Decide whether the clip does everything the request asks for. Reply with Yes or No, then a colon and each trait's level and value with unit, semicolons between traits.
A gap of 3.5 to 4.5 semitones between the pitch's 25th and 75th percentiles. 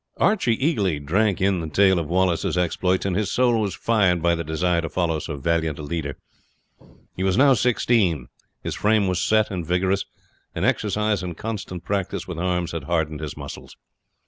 Yes: average, 3.8 semitones